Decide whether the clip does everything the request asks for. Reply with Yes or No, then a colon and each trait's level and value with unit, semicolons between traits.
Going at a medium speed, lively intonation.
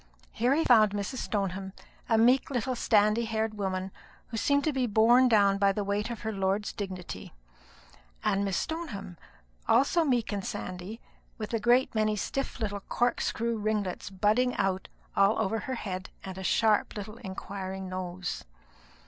No: average, 160 wpm; average, 3.3 semitones